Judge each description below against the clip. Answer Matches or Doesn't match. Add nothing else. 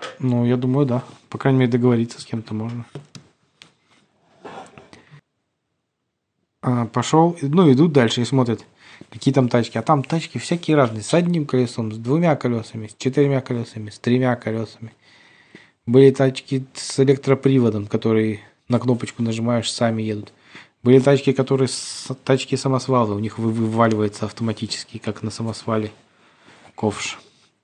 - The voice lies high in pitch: Doesn't match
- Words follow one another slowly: Doesn't match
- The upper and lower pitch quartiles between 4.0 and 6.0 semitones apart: Doesn't match